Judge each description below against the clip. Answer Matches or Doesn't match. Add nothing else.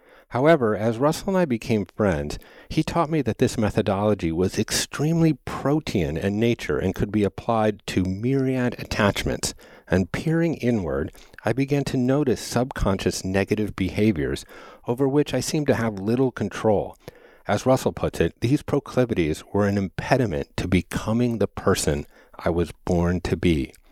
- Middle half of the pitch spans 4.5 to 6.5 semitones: Matches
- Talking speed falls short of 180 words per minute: Matches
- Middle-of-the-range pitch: Doesn't match